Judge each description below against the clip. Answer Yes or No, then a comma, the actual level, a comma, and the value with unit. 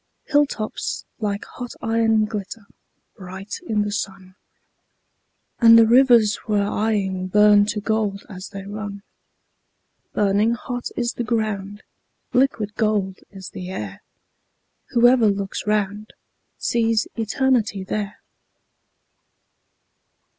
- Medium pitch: No, high, 210 Hz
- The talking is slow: Yes, slow, 110 wpm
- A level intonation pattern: Yes, narrow, 2.2 semitones